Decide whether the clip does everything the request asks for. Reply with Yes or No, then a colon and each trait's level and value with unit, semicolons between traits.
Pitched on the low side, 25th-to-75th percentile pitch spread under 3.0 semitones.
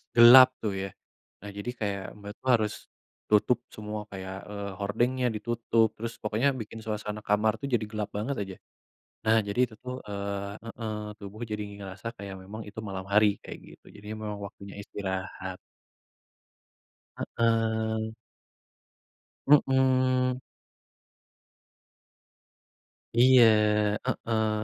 Yes: low, 110 Hz; narrow, 2.4 semitones